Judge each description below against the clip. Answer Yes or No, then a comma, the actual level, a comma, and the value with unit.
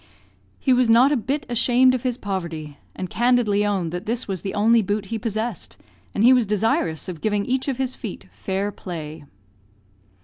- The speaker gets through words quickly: No, average, 190 wpm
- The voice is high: Yes, high, 215 Hz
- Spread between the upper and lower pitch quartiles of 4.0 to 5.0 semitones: Yes, average, 4.5 semitones